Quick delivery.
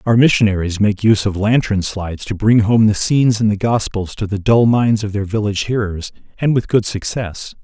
Yes: fast, 210 wpm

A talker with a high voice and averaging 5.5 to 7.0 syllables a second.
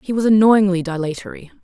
Yes: high, 195 Hz; 6.3 syllables/s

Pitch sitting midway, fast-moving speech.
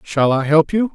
Yes: medium, 165 Hz; fast, 255 wpm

